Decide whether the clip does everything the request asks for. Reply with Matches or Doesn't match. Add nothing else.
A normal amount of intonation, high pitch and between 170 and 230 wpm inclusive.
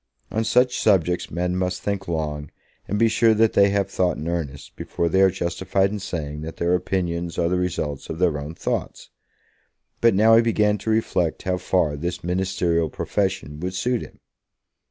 Doesn't match